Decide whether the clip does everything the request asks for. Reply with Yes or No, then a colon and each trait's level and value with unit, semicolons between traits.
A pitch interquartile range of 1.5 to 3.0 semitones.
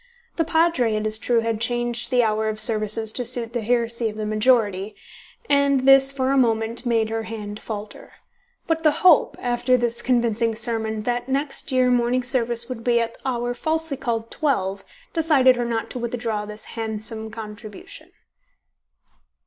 Yes: narrow, 2.5 semitones